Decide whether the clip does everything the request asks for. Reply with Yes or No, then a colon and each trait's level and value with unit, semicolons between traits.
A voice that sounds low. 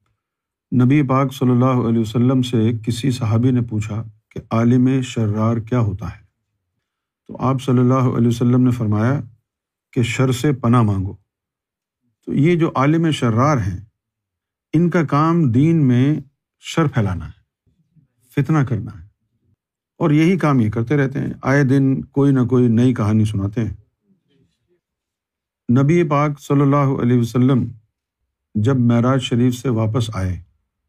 Yes: low, 125 Hz